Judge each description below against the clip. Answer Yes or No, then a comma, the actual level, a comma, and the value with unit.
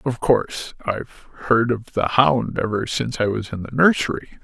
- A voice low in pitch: Yes, low, 120 Hz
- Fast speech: No, average, 190 wpm